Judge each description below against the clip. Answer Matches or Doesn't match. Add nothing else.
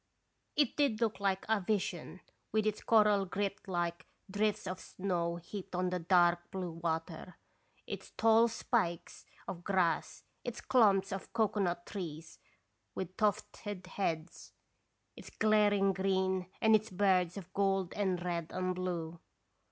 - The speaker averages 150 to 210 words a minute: Doesn't match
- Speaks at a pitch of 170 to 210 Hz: Matches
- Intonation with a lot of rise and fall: Doesn't match